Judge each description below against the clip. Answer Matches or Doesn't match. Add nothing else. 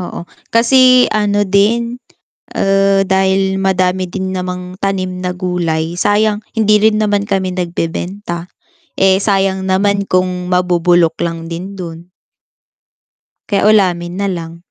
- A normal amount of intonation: Doesn't match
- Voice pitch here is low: Doesn't match